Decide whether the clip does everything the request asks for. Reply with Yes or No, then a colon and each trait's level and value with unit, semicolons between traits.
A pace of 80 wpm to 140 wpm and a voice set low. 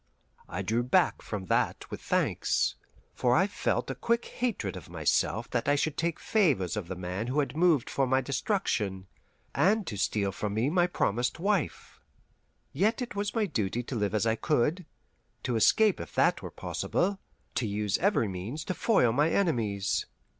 No: average, 180 wpm; low, 130 Hz